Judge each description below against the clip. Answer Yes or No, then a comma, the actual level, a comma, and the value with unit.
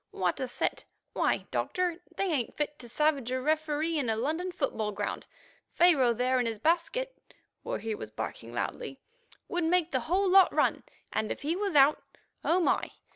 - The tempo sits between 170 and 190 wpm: Yes, average, 180 wpm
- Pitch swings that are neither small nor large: No, wide, 6.5 semitones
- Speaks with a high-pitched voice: Yes, very high, 295 Hz